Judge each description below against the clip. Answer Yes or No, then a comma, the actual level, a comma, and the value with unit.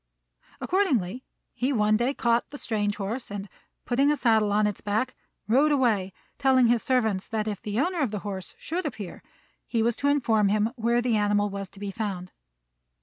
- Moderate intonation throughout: Yes, average, 3.9 semitones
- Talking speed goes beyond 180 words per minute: Yes, average, 190 wpm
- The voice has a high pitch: Yes, high, 220 Hz